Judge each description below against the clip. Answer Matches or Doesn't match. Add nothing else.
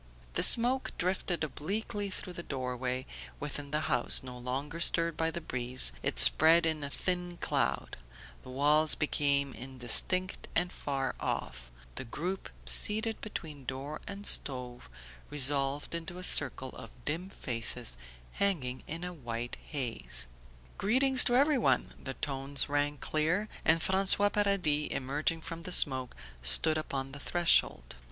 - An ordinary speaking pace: Matches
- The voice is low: Doesn't match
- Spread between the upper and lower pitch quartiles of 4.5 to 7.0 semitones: Matches